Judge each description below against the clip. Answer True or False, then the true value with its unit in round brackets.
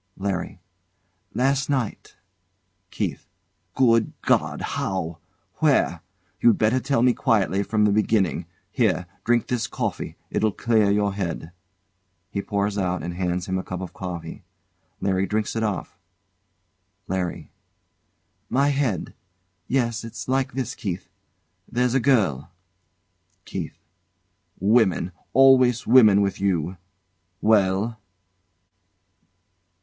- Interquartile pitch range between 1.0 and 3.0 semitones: False (4.2 semitones)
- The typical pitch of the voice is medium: False (105 Hz)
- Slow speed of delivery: True (115 wpm)